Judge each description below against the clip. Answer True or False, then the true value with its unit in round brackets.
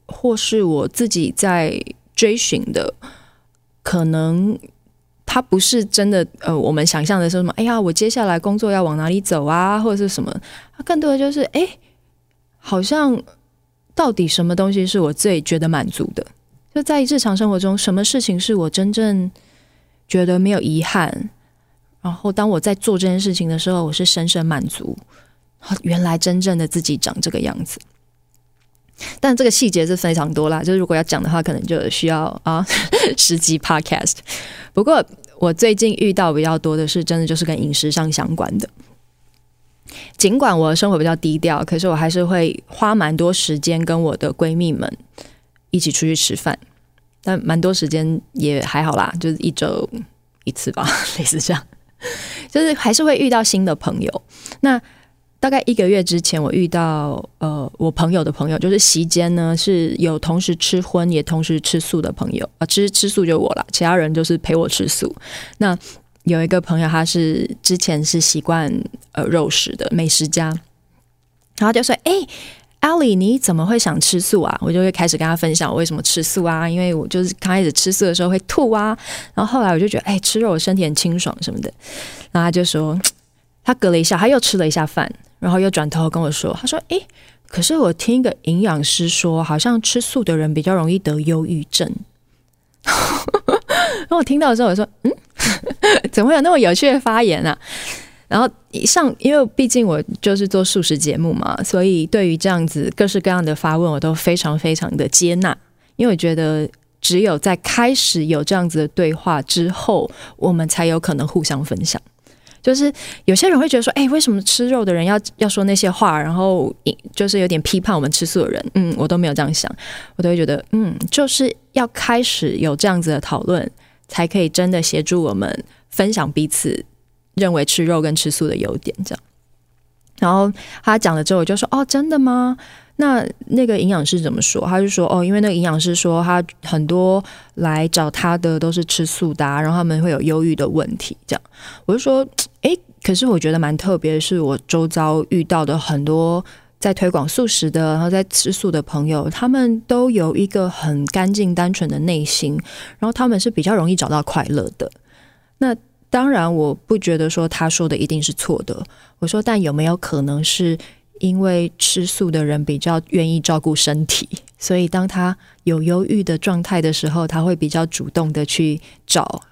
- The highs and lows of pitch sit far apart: False (4.2 semitones)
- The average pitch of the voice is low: False (175 Hz)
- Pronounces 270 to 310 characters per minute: True (285 characters per minute)